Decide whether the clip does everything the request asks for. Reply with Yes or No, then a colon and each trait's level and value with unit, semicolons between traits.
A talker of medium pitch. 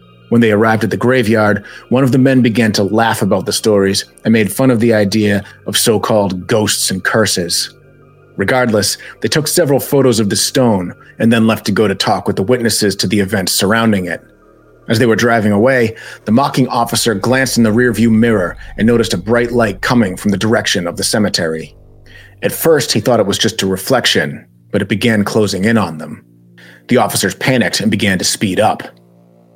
No: low, 110 Hz